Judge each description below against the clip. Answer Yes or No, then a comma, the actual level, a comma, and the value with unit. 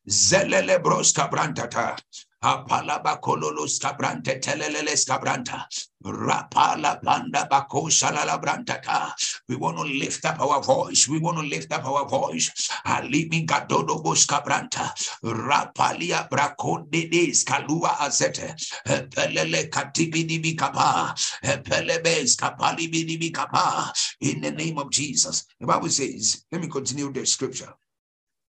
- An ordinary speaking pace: No, slow, 100 wpm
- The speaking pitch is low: No, medium, 155 Hz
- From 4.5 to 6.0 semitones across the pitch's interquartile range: No, average, 3.2 semitones